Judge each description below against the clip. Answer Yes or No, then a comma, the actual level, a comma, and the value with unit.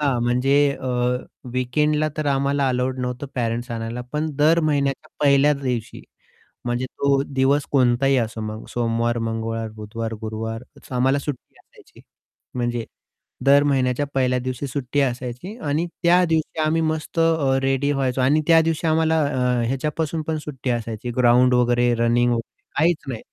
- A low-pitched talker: Yes, low, 130 Hz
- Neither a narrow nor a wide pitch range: Yes, average, 3.3 semitones